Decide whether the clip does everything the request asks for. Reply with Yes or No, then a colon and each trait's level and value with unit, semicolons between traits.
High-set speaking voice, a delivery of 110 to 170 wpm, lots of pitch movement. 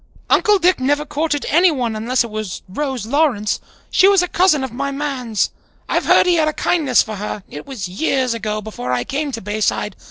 No: very high, 260 Hz; average, 200 wpm; wide, 5.9 semitones